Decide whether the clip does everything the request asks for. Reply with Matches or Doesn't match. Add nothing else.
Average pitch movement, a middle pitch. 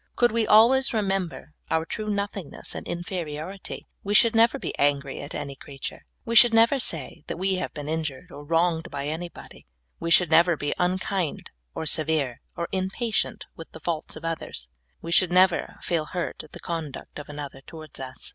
Matches